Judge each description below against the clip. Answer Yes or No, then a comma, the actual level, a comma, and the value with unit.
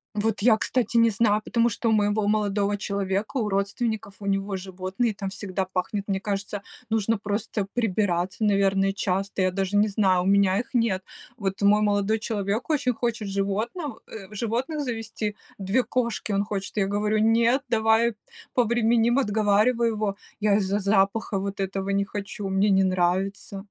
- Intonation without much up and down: Yes, narrow, 2.3 semitones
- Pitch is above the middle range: Yes, high, 205 Hz